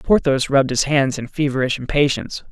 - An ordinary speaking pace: Yes, average, 165 wpm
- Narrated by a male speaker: Yes, male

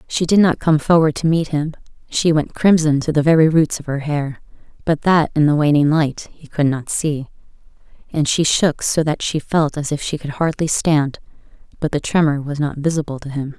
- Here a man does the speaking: No, female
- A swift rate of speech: Yes, fast, 215 wpm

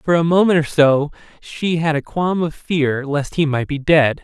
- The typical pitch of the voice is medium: Yes, medium, 155 Hz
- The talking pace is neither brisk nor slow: No, fast, 225 wpm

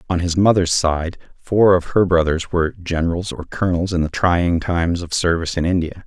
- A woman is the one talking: No, male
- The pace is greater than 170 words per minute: Yes, average, 200 wpm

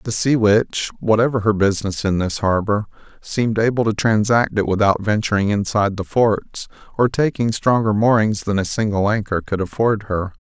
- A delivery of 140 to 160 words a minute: No, average, 170 wpm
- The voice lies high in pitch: No, low, 105 Hz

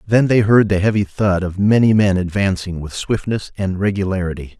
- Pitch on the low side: Yes, low, 100 Hz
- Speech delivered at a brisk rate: No, average, 185 wpm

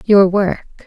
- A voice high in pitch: Yes, high, 195 Hz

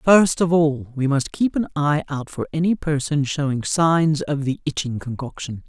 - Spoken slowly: No, average, 190 wpm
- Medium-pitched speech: Yes, medium, 150 Hz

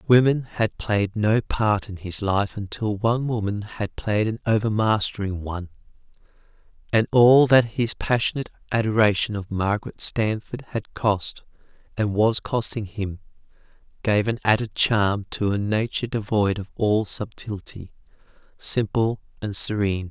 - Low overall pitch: Yes, low, 105 Hz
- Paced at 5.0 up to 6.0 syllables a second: No, 4.5 syllables/s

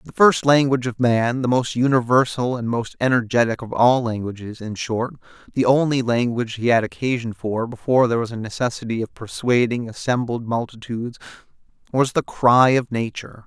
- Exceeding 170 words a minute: No, average, 165 wpm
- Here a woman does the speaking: No, male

